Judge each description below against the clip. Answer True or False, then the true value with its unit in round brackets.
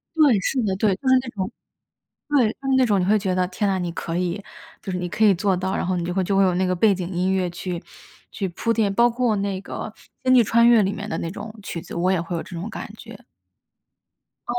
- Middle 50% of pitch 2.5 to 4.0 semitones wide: True (3.3 semitones)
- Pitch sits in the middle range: False (195 Hz)